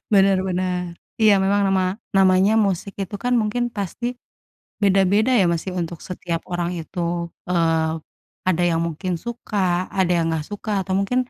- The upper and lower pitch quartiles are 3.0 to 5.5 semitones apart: No, narrow, 2.6 semitones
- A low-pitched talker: No, high, 190 Hz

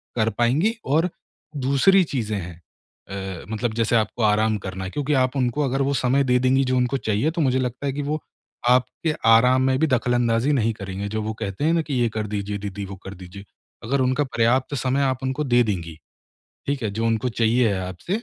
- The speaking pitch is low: Yes, low, 120 Hz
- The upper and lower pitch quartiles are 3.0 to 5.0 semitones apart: Yes, average, 4.2 semitones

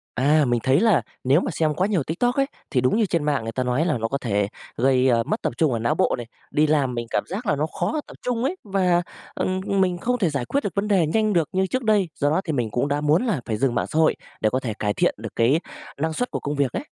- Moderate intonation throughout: No, wide, 7.0 semitones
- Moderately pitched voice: Yes, medium, 150 Hz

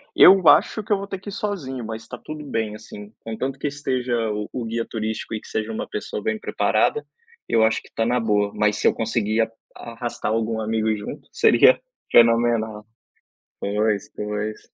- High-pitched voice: No, low, 115 Hz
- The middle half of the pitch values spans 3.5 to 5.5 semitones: No, average, 2.8 semitones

